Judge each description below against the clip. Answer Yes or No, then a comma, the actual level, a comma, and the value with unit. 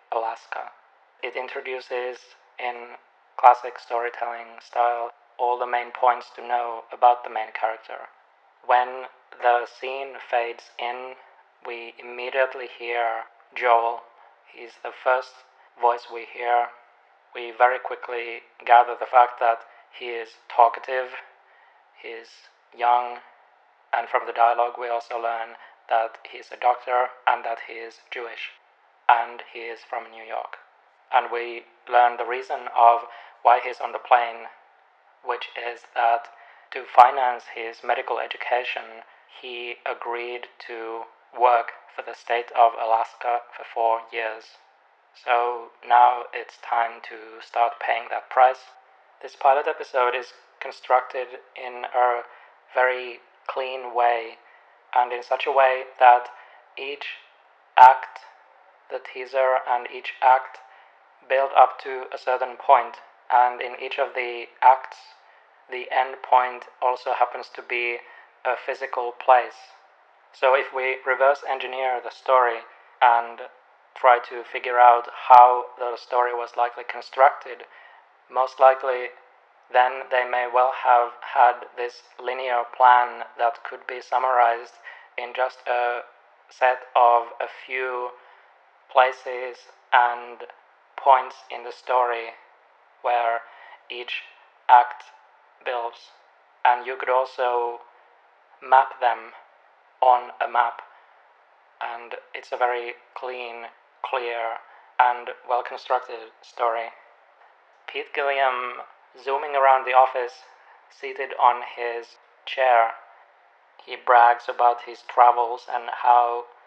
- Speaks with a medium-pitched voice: No, low, 120 Hz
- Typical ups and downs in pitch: No, narrow, 1.2 semitones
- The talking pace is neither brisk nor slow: No, slow, 120 wpm